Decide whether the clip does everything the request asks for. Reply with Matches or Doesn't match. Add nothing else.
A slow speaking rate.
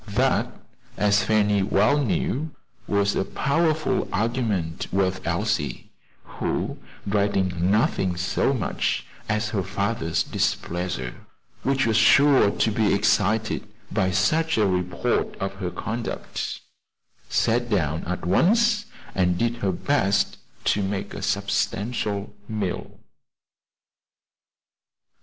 Matches